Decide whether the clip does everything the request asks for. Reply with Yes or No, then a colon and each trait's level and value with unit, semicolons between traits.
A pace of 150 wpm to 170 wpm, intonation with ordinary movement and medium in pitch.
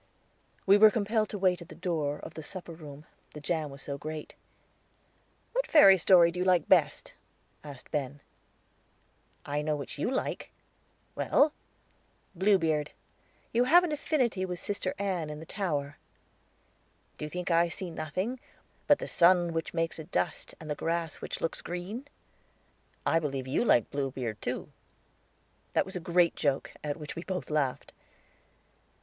Yes: average, 160 wpm; average, 4.1 semitones; medium, 170 Hz